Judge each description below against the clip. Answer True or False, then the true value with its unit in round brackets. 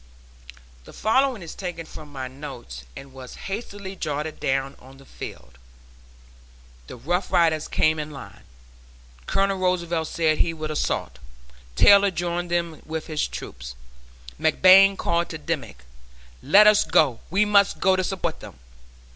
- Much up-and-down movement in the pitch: False (4.3 semitones)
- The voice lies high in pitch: False (165 Hz)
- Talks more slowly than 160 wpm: True (145 wpm)